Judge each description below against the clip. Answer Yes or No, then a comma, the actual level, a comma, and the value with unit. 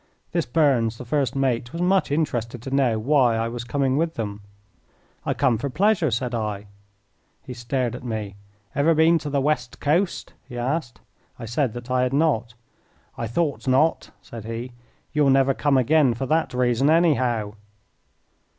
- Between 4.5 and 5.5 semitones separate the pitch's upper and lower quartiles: No, average, 4.0 semitones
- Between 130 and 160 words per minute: No, average, 170 wpm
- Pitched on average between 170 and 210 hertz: No, low, 130 Hz